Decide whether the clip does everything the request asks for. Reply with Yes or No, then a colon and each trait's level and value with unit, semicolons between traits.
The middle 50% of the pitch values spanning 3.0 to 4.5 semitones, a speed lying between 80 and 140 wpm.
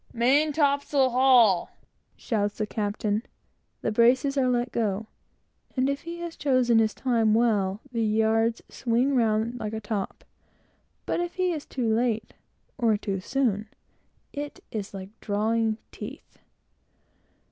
Yes: average, 3.5 semitones; slow, 135 wpm